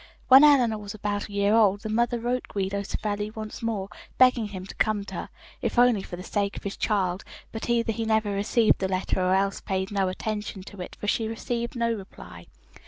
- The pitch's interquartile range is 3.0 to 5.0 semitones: No, narrow, 2.6 semitones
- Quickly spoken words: Yes, fast, 220 wpm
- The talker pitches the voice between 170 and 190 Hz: No, high, 210 Hz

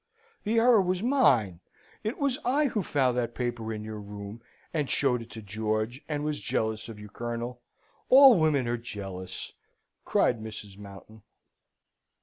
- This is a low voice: Yes, low, 120 Hz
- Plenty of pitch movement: Yes, wide, 6.6 semitones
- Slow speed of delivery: No, average, 155 wpm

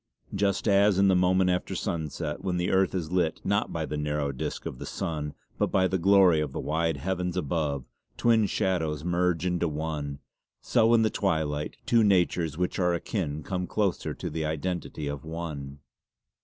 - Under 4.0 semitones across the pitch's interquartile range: Yes, average, 3.6 semitones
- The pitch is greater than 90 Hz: No, very low, 85 Hz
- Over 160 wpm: Yes, average, 185 wpm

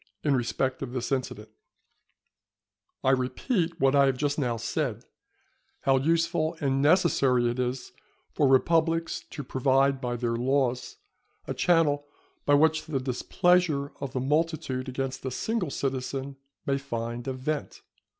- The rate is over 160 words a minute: No, average, 140 wpm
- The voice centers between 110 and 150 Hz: Yes, low, 135 Hz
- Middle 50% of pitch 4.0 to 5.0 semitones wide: No, average, 3.2 semitones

